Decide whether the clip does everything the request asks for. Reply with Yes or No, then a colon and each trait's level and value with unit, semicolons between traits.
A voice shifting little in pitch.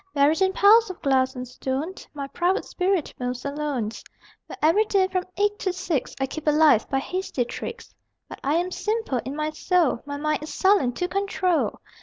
No: wide, 5.6 semitones